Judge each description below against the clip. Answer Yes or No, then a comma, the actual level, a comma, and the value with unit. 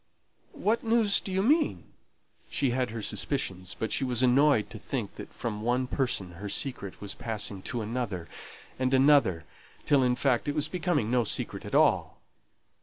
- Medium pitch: No, low, 125 Hz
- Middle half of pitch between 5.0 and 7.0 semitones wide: Yes, wide, 5.4 semitones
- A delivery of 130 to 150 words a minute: No, average, 175 wpm